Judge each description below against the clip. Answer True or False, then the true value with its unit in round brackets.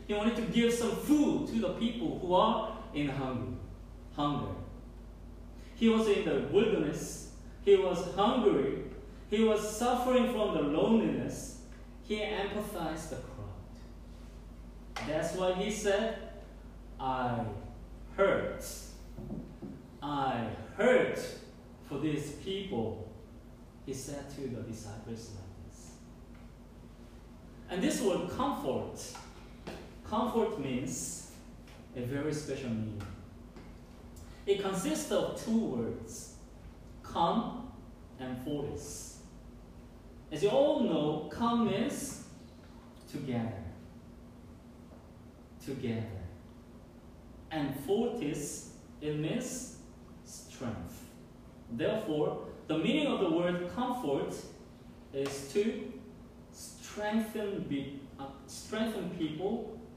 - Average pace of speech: False (95 wpm)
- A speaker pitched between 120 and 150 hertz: True (140 Hz)